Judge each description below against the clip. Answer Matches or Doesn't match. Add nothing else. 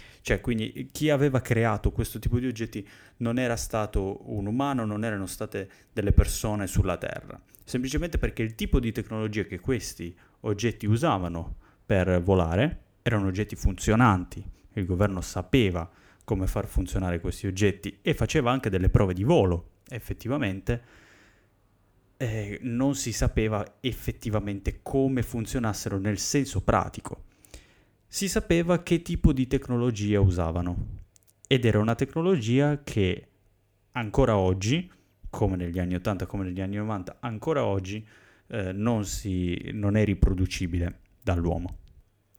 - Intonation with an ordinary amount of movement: Matches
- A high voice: Doesn't match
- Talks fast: Doesn't match